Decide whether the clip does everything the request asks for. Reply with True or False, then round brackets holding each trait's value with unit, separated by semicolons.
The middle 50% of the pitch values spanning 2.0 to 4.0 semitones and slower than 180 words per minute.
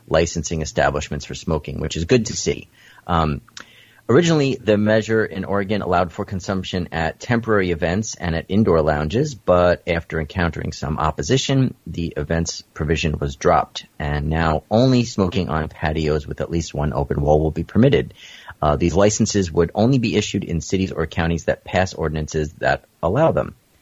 False (4.8 semitones; 170 wpm)